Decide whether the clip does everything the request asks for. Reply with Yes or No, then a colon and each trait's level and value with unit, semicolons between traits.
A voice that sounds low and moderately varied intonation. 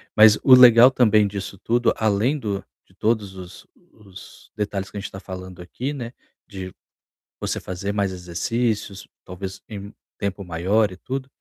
Yes: low, 100 Hz; average, 3.4 semitones